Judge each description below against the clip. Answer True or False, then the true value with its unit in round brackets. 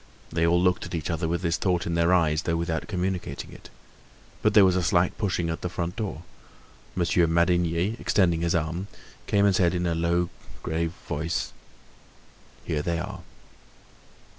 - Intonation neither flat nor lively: False (1.6 semitones)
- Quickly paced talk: False (175 wpm)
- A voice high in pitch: False (85 Hz)